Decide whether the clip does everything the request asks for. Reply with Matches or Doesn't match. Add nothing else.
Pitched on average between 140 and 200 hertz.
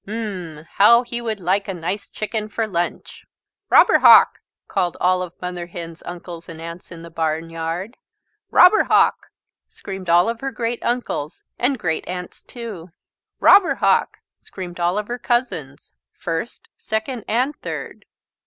Matches